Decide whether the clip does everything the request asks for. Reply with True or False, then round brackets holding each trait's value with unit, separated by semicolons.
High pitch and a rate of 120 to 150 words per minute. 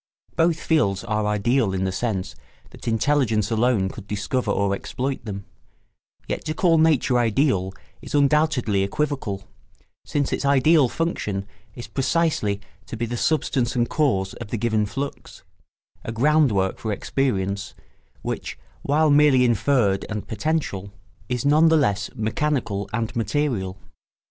False (120 Hz; 140 wpm)